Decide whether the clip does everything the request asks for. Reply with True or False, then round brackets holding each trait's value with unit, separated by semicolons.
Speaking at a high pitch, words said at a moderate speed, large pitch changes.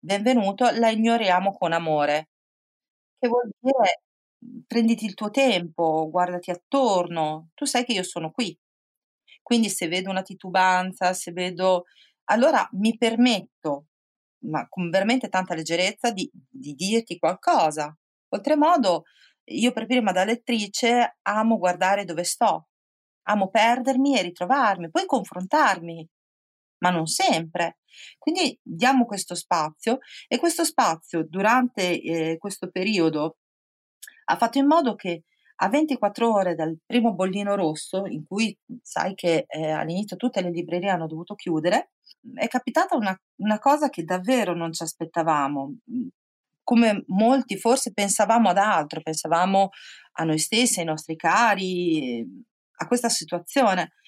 True (195 Hz; 135 wpm; 5.8 semitones)